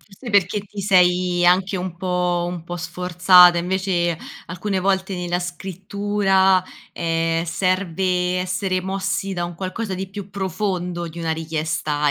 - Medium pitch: Yes, medium, 180 Hz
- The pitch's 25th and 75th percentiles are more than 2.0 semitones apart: No, narrow, 1.7 semitones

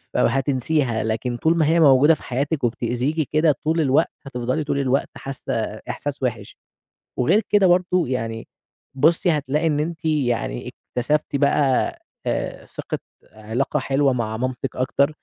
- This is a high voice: No, medium, 140 Hz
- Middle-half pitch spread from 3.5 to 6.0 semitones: Yes, average, 3.9 semitones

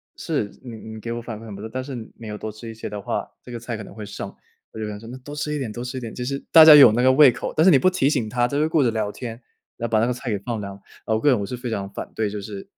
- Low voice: Yes, low, 115 Hz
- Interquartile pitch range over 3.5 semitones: No, average, 3.2 semitones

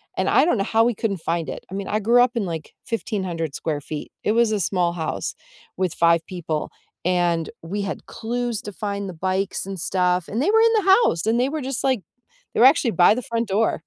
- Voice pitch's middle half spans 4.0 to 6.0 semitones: Yes, average, 5.1 semitones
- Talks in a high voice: Yes, high, 200 Hz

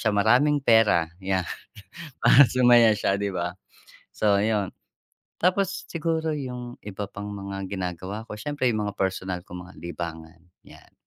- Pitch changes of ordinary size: Yes, average, 4.8 semitones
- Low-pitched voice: Yes, low, 105 Hz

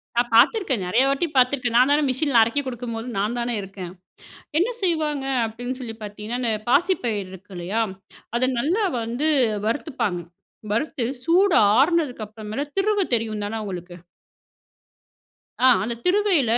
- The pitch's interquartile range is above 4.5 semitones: Yes, average, 5.3 semitones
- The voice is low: No, high, 245 Hz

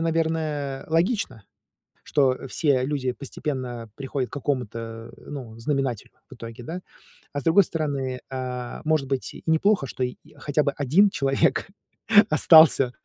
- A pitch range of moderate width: Yes, average, 3.7 semitones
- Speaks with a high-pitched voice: No, medium, 140 Hz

